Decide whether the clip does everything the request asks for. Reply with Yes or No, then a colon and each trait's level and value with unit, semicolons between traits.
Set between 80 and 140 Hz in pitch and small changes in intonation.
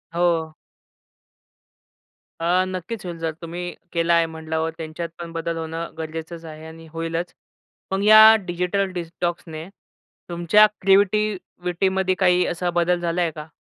No: medium, 170 Hz; narrow, 1.7 semitones